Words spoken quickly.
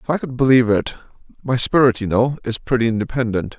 No: average, 185 wpm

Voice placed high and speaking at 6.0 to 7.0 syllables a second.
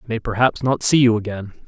No: low, 115 Hz; 6.4 syllables/s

